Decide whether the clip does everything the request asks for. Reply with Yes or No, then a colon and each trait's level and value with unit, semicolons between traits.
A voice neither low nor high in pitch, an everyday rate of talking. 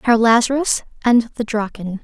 No: high, 230 Hz; average, 150 wpm